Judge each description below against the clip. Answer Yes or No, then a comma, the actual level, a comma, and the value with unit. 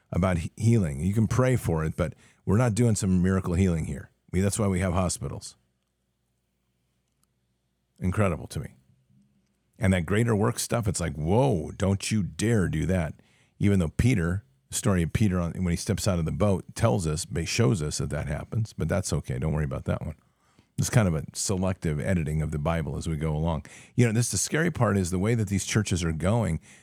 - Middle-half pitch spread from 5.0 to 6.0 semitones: Yes, average, 5.3 semitones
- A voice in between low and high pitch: No, very low, 95 Hz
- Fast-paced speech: Yes, fast, 210 wpm